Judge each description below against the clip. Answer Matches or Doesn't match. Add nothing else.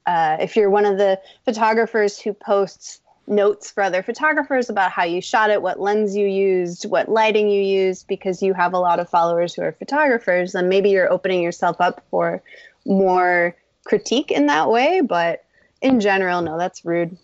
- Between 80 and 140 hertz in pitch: Doesn't match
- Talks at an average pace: Matches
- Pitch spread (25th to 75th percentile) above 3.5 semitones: Doesn't match